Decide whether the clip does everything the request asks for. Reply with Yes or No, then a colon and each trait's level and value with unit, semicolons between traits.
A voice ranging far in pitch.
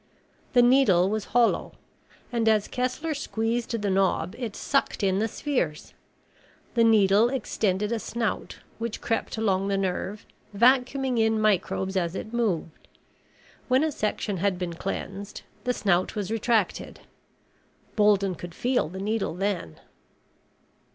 No: average, 3.6 semitones